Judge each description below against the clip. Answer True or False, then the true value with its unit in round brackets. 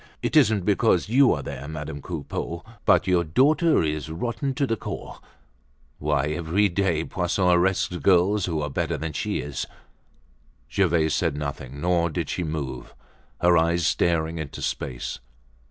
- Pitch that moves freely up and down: False (3.9 semitones)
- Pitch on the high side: False (85 Hz)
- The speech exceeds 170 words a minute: False (155 wpm)